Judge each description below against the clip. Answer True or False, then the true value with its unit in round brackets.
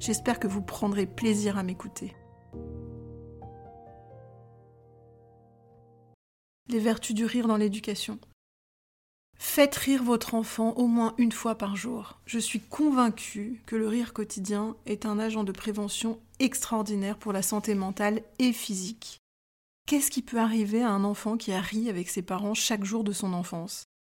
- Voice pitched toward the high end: True (210 Hz)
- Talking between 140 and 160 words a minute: True (150 wpm)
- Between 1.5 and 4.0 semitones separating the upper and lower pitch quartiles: True (3.5 semitones)